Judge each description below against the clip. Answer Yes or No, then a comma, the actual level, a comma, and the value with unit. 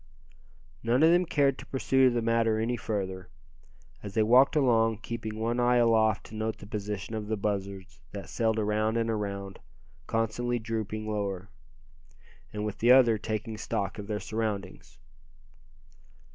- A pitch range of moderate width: No, narrow, 2.0 semitones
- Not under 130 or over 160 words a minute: Yes, average, 155 wpm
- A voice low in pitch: Yes, low, 110 Hz